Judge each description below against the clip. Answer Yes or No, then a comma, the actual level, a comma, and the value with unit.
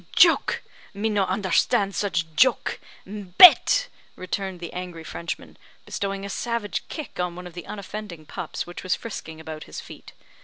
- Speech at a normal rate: Yes, average, 155 wpm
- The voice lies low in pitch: No, high, 190 Hz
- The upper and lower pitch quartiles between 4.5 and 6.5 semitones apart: No, average, 2.8 semitones